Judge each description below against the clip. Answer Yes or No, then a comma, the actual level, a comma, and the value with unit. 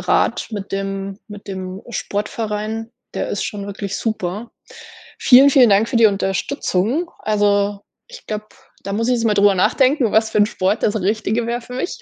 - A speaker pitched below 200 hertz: No, high, 210 Hz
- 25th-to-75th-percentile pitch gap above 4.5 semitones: No, average, 2.7 semitones